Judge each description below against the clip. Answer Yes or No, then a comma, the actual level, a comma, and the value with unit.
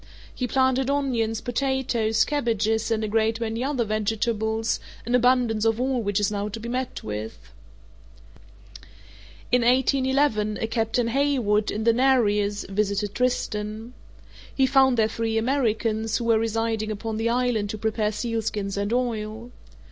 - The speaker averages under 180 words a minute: Yes, average, 145 wpm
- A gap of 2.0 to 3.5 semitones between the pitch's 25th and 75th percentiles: Yes, narrow, 2.6 semitones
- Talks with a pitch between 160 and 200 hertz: No, high, 225 Hz